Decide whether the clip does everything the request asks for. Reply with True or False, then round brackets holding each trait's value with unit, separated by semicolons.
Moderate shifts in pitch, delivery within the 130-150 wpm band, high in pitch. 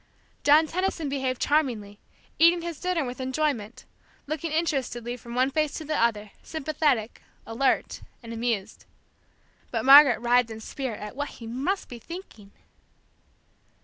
True (5.0 semitones; 140 wpm; 260 Hz)